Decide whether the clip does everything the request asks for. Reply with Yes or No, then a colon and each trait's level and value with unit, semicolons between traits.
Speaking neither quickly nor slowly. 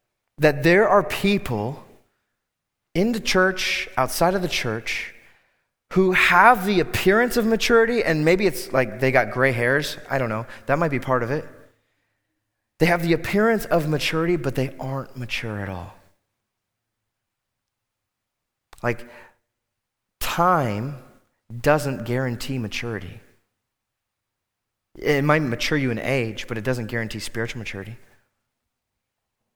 No: slow, 130 wpm